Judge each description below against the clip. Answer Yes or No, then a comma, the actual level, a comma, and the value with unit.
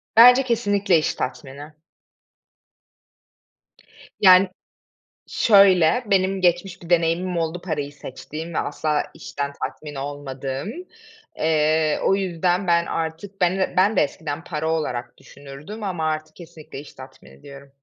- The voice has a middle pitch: Yes, medium, 165 Hz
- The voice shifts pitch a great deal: No, average, 4.2 semitones